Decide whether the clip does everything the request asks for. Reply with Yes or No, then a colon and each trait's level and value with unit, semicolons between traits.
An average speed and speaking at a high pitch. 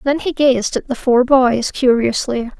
Yes: average, 185 wpm; very high, 255 Hz